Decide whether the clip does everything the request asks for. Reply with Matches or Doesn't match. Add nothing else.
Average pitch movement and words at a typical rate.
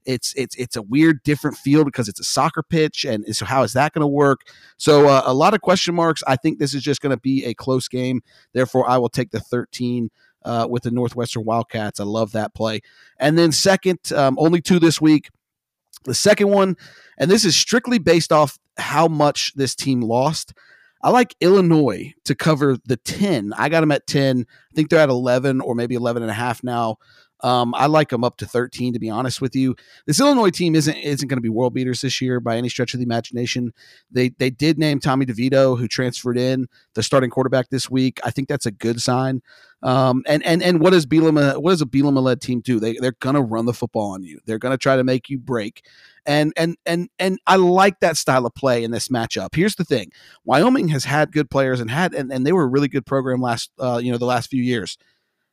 Doesn't match